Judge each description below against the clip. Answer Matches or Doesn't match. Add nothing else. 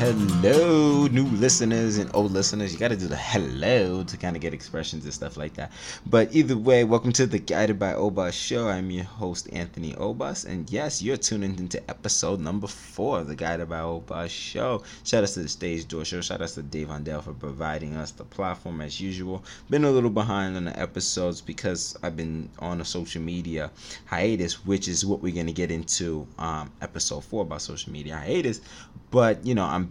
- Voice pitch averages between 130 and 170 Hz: Doesn't match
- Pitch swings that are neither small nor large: Matches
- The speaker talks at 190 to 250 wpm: Matches